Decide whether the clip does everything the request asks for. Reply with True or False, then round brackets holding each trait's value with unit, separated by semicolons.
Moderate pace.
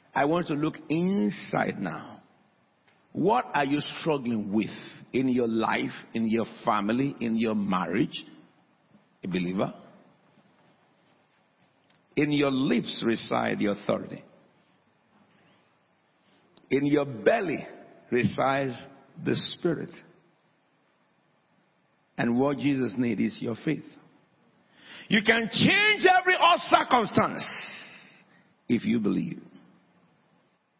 False (95 wpm)